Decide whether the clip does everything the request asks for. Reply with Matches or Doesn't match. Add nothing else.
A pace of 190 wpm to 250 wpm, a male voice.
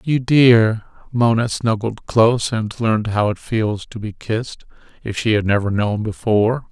Doesn't match